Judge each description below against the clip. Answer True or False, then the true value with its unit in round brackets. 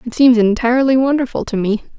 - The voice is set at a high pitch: True (240 Hz)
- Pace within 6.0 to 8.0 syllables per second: True (6.3 syllables/s)